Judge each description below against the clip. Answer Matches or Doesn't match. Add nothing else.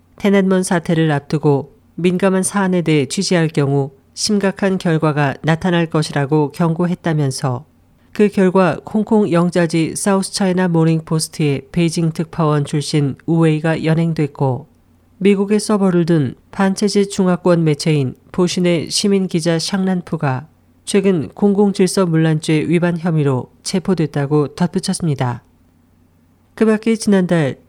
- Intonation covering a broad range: Doesn't match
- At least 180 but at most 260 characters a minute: Doesn't match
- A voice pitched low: Doesn't match